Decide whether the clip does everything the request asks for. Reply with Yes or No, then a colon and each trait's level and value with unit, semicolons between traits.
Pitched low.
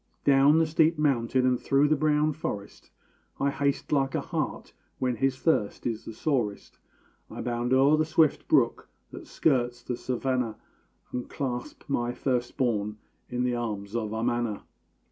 Yes: low, 125 Hz